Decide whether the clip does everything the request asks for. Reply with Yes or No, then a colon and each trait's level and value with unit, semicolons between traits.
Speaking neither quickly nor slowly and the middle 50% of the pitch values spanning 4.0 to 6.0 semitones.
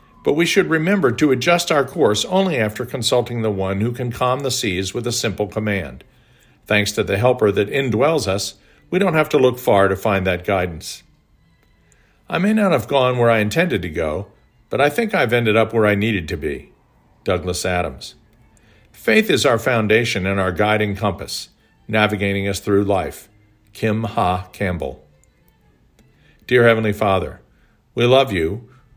Yes: average, 170 wpm; average, 4.3 semitones